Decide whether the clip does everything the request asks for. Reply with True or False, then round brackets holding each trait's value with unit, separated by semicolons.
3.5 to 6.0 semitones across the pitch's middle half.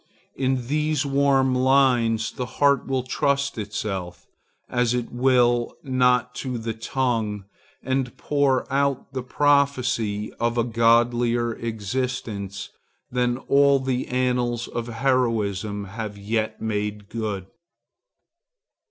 False (2.9 semitones)